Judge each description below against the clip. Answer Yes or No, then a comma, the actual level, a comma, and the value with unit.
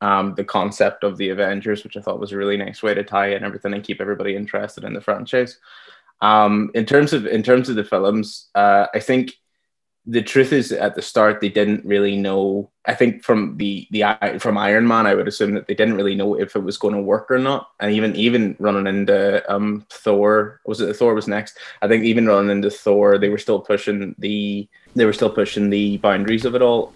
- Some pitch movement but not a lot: No, narrow, 1.6 semitones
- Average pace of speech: No, fast, 230 wpm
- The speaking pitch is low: Yes, low, 105 Hz